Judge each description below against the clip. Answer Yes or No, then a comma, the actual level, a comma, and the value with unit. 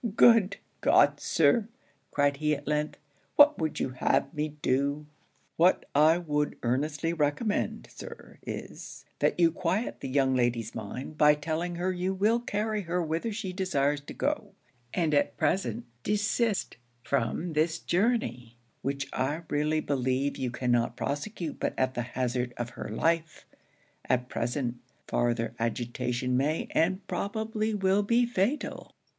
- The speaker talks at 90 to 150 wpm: Yes, average, 145 wpm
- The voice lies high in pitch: No, medium, 150 Hz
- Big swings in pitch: Yes, wide, 6.3 semitones